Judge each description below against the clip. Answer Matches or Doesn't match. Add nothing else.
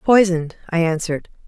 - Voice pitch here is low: Doesn't match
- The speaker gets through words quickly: Doesn't match